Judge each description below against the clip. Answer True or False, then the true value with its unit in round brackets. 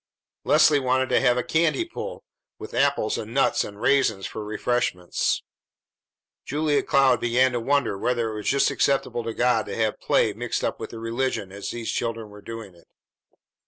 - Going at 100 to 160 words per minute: False (185 wpm)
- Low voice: True (120 Hz)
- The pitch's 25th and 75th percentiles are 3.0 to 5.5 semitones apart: True (3.7 semitones)